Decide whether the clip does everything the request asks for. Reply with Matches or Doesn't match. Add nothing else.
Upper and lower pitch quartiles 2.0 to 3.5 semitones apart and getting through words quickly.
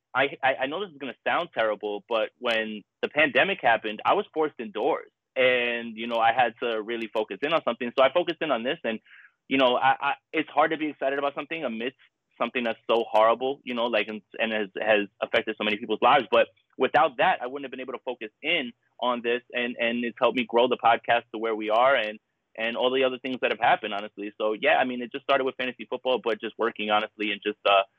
Matches